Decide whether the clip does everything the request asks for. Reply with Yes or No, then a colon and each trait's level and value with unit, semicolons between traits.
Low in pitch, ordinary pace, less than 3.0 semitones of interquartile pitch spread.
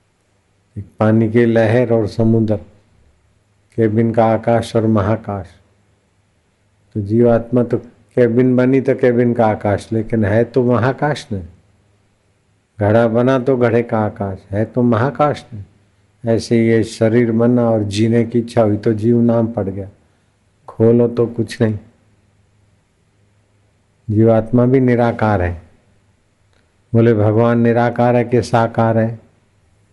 Yes: low, 110 Hz; average, 130 wpm; narrow, 2.6 semitones